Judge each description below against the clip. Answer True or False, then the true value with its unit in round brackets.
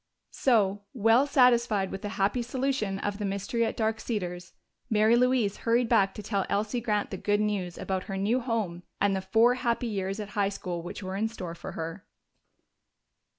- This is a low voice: False (210 Hz)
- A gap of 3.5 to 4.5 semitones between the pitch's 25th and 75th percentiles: False (3.1 semitones)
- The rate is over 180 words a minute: True (190 wpm)